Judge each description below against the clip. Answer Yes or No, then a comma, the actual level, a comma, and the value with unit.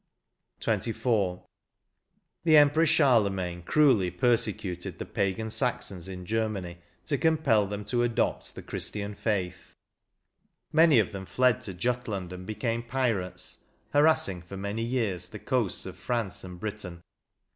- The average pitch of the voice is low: Yes, low, 105 Hz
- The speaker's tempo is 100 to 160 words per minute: Yes, slow, 135 wpm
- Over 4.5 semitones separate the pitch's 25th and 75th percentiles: Yes, average, 4.9 semitones